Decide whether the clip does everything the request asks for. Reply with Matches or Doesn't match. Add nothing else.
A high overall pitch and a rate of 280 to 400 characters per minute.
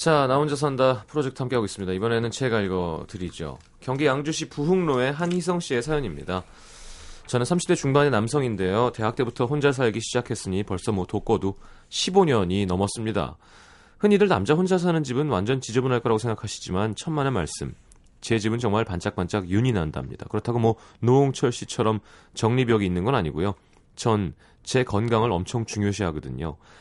Doesn't match